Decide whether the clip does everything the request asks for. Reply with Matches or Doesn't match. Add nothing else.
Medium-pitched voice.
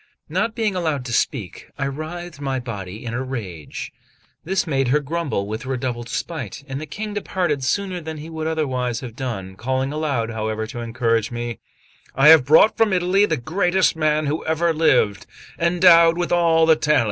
Matches